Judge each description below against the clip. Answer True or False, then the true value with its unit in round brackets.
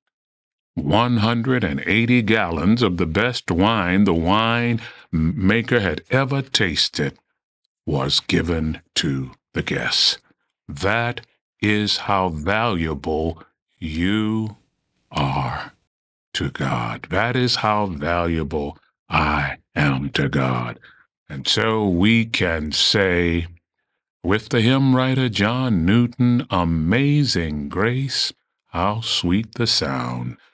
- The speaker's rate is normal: False (100 wpm)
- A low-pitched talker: True (100 Hz)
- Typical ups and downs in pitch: False (6.1 semitones)